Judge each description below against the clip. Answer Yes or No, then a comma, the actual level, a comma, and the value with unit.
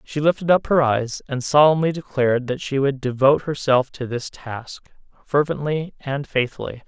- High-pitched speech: No, medium, 140 Hz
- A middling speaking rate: Yes, average, 165 wpm